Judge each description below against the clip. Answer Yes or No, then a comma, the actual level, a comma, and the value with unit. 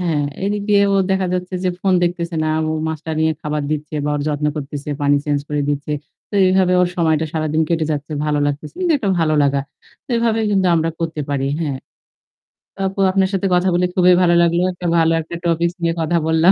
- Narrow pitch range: No, average, 3.2 semitones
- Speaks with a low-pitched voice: No, medium, 165 Hz